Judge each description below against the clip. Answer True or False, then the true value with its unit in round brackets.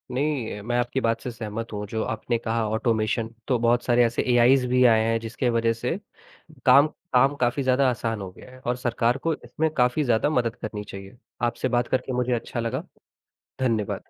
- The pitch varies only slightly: True (2.0 semitones)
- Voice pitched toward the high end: False (120 Hz)